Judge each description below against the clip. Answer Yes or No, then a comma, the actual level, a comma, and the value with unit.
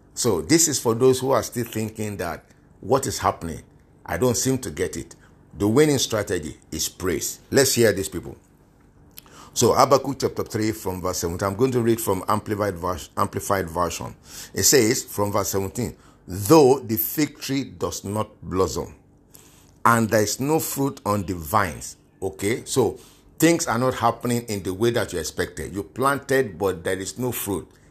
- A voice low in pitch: Yes, low, 110 Hz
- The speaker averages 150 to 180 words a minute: Yes, average, 175 wpm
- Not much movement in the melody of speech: No, average, 4.6 semitones